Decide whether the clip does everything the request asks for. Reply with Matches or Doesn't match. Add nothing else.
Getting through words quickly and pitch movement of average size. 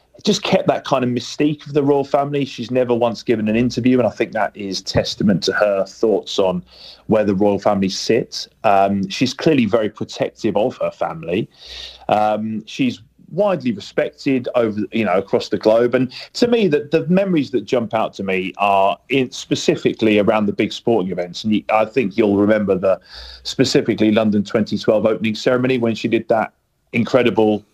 Doesn't match